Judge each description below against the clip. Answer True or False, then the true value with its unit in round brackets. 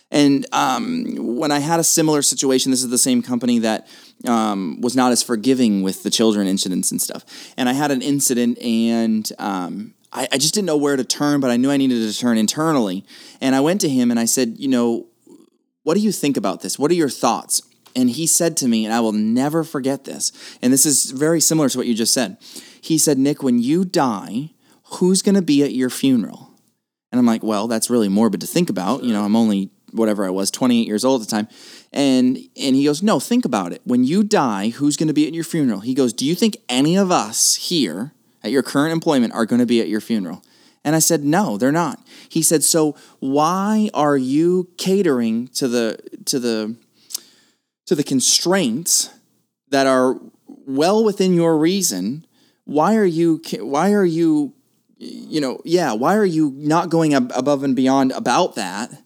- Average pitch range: False (6.0 semitones)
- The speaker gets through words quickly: True (210 wpm)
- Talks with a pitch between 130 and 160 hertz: True (140 Hz)